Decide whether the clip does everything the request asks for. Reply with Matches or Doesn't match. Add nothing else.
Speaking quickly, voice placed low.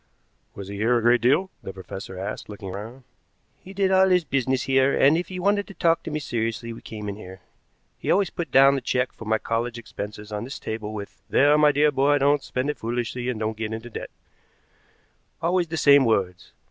Matches